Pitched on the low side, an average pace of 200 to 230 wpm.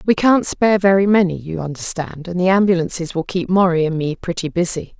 No: medium, 180 Hz; fast, 205 wpm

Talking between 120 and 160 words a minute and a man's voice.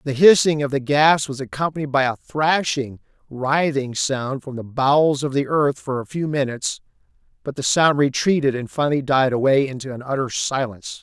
No: average, 185 wpm; male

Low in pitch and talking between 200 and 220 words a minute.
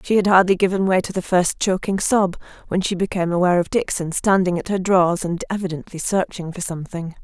No: medium, 185 Hz; fast, 205 wpm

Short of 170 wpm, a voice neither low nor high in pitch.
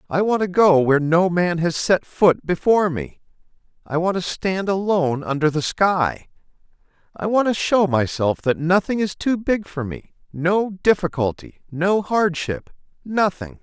Yes: average, 155 wpm; medium, 175 Hz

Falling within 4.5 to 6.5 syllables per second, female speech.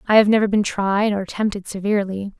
Yes: 6.0 syllables/s; female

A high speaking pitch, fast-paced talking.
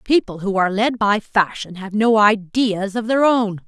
No: high, 210 Hz; average, 195 wpm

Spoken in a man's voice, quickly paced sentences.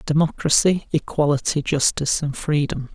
No: male; slow, 100 wpm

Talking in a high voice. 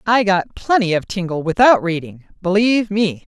Yes: high, 195 Hz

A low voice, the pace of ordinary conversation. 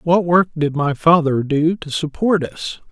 No: medium, 160 Hz; average, 185 wpm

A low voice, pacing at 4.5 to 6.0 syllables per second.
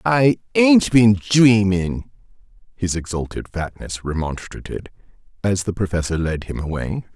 No: low, 100 Hz; 4.2 syllables/s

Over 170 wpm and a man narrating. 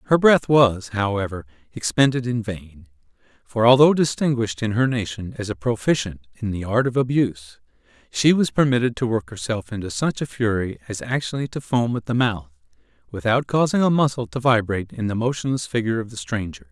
Yes: average, 185 wpm; male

